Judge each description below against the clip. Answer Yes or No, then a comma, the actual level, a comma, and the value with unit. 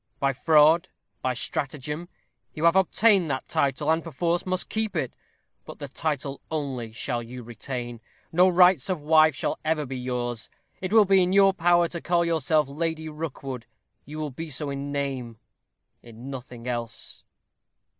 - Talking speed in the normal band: Yes, average, 165 wpm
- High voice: No, medium, 150 Hz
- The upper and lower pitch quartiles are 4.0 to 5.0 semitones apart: Yes, average, 4.7 semitones